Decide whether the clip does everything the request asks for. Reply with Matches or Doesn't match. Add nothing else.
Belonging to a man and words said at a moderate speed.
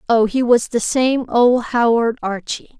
Doesn't match